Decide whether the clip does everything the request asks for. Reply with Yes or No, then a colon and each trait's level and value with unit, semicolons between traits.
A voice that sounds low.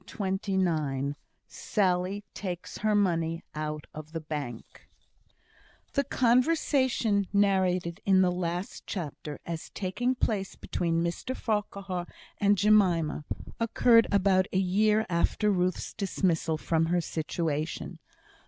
No: medium, 185 Hz